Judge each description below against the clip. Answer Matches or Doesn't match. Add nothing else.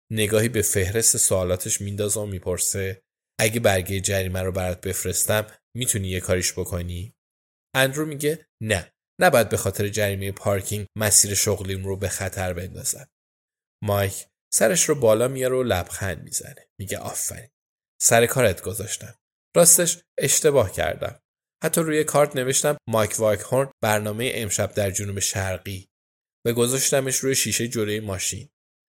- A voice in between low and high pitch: Doesn't match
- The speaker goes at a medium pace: Matches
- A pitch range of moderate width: Matches